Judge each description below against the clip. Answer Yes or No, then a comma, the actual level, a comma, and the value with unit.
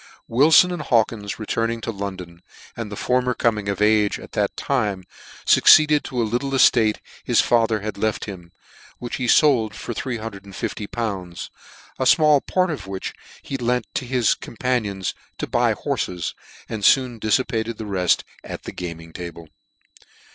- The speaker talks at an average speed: Yes, average, 155 wpm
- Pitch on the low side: Yes, low, 110 Hz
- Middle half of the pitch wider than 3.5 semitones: Yes, average, 3.9 semitones